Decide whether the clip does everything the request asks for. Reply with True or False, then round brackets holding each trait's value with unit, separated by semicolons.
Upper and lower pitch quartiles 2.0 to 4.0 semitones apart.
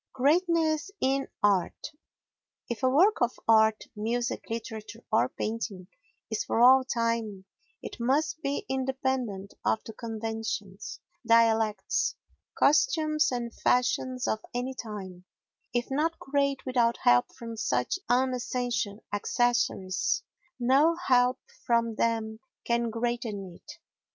True (3.2 semitones)